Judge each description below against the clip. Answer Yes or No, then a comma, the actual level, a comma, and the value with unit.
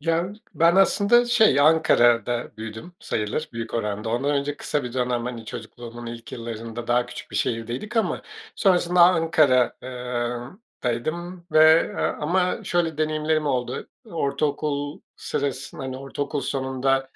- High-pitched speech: No, low, 135 Hz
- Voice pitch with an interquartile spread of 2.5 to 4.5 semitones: No, average, 5.1 semitones